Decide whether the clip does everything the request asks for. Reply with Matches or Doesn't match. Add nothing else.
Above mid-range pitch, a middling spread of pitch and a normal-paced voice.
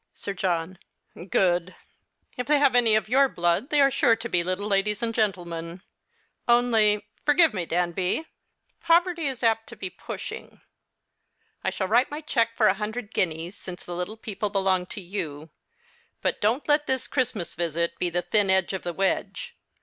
Matches